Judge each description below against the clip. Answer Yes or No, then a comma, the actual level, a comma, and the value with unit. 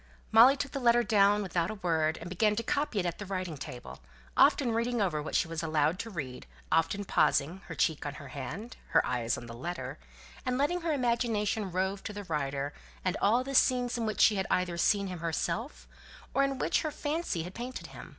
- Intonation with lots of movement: Yes, wide, 6.6 semitones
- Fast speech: Yes, fast, 220 wpm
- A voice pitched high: Yes, high, 195 Hz